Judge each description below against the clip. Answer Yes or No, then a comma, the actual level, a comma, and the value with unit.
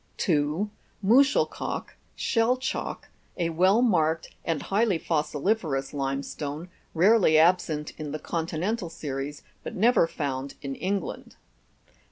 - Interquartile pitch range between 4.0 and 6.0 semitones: Yes, average, 5.3 semitones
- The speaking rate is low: Yes, slow, 115 wpm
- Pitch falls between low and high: Yes, medium, 165 Hz